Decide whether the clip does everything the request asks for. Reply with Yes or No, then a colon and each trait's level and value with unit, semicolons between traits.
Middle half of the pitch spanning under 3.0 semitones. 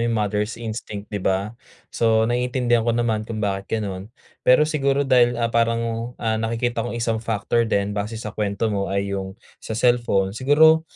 Yes: narrow, 2.6 semitones